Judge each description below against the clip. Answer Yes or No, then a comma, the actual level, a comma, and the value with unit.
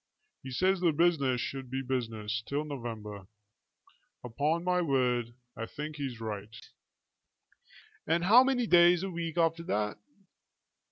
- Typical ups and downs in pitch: No, wide, 6.4 semitones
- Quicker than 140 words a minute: No, slow, 135 wpm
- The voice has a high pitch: No, medium, 140 Hz